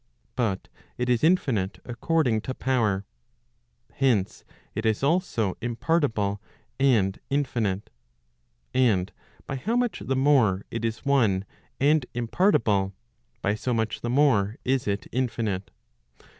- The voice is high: No, low, 120 Hz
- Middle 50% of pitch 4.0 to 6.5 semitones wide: Yes, average, 4.8 semitones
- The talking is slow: Yes, slow, 130 wpm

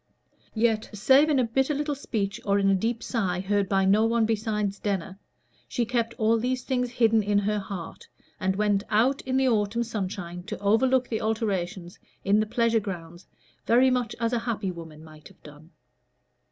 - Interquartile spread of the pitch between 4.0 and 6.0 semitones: No, average, 3.3 semitones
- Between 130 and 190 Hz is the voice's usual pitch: No, high, 215 Hz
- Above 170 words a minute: Yes, average, 185 wpm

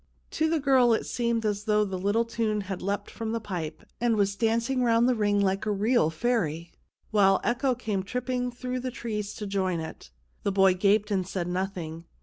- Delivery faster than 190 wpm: Yes, average, 200 wpm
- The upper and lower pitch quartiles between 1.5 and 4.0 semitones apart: Yes, average, 3.5 semitones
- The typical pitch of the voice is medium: No, high, 210 Hz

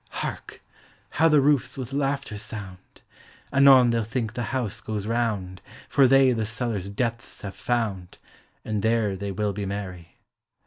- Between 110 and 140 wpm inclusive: No, average, 150 wpm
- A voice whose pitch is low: Yes, low, 110 Hz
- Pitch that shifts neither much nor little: Yes, average, 4.1 semitones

